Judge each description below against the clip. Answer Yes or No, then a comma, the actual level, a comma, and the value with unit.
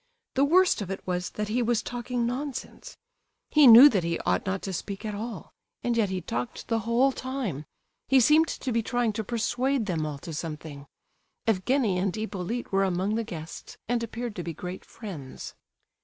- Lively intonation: No, average, 4.9 semitones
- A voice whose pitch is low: No, high, 220 Hz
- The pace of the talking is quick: No, average, 190 wpm